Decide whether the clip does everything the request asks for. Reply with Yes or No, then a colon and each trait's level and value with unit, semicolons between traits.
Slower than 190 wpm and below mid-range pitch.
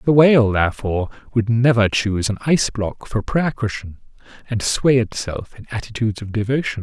Yes: average, 165 wpm; low, 115 Hz